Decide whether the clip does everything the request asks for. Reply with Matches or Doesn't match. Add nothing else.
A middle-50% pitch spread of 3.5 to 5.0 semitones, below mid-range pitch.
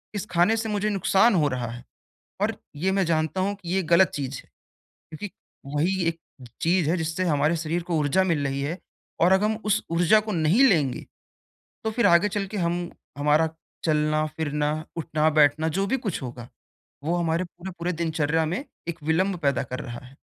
Doesn't match